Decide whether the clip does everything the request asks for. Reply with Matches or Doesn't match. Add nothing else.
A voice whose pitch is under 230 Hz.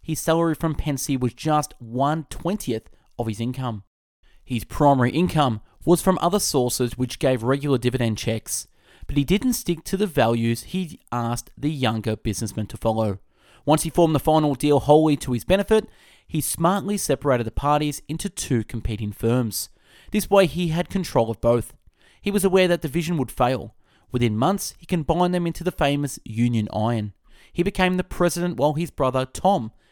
Matches